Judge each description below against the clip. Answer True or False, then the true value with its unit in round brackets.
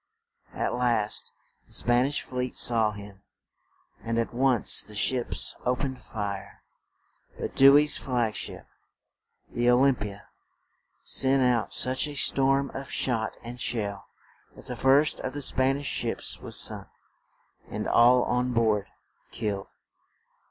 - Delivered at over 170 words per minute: False (145 wpm)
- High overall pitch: False (125 Hz)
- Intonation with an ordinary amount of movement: True (3.2 semitones)